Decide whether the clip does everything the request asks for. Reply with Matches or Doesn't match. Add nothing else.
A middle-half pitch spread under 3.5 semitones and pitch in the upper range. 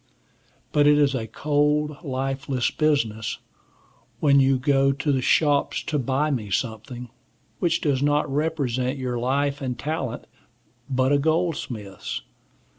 Doesn't match